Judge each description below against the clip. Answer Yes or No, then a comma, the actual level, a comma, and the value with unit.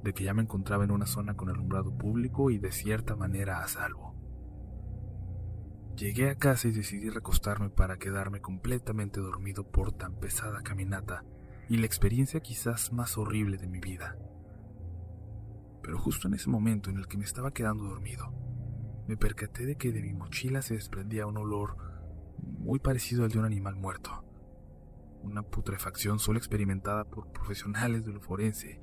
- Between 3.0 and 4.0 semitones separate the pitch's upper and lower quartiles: No, narrow, 2.4 semitones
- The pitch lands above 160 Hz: No, low, 105 Hz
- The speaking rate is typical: Yes, average, 165 wpm